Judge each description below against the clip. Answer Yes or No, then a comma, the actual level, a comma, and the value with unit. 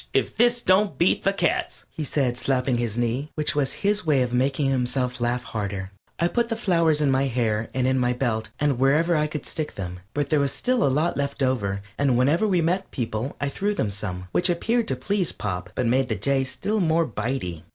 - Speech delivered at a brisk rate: Yes, fast, 225 wpm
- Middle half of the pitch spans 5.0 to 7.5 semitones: Yes, wide, 5.6 semitones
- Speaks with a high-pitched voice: No, low, 135 Hz